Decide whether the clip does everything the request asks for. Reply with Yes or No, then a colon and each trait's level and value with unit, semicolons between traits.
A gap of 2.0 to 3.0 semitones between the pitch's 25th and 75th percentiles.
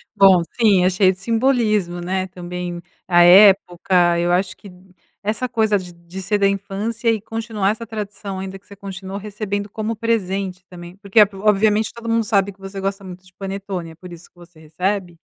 Yes: narrow, 2.6 semitones